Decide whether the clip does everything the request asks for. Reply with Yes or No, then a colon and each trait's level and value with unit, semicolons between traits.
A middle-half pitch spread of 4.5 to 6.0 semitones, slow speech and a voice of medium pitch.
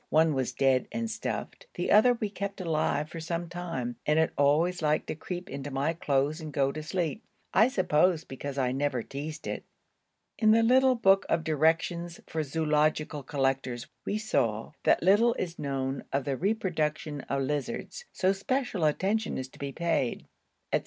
No: average, 5.0 semitones; average, 175 wpm; medium, 155 Hz